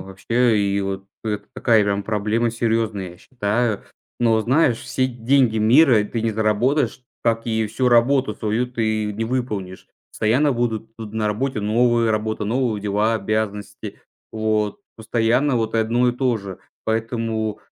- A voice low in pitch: Yes, low, 110 Hz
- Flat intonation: Yes, narrow, 2.2 semitones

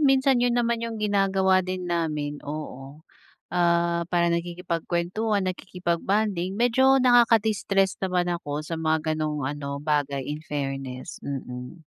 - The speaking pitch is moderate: Yes, medium, 175 Hz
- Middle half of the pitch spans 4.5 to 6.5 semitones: Yes, average, 5.1 semitones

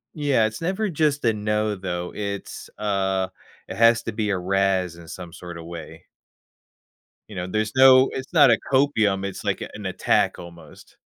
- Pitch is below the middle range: Yes, low, 105 Hz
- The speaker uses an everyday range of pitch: Yes, average, 4.7 semitones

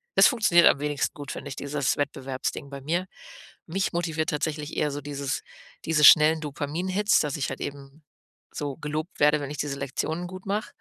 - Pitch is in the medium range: Yes, medium, 150 Hz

